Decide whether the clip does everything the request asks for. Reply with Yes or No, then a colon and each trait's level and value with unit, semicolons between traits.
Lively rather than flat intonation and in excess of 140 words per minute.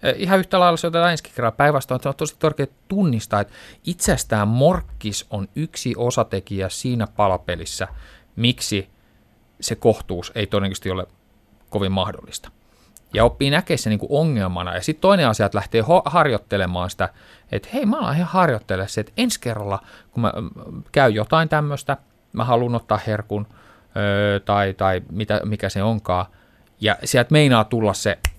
Yes: wide, 5.9 semitones; average, 150 wpm